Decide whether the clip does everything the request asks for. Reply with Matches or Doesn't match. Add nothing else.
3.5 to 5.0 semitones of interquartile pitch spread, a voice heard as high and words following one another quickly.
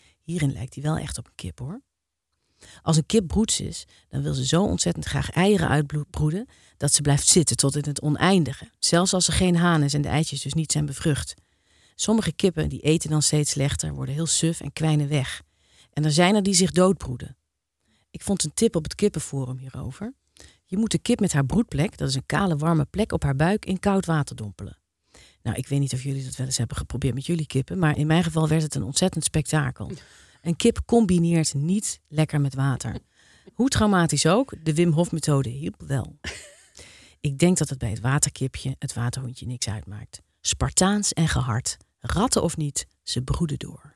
Doesn't match